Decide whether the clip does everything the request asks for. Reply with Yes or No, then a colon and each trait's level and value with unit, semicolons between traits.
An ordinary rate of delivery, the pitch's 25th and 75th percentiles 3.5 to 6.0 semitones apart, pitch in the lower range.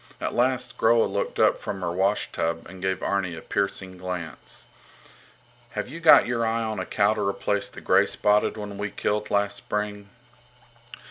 No: average, 170 wpm; narrow, 2.5 semitones; low, 100 Hz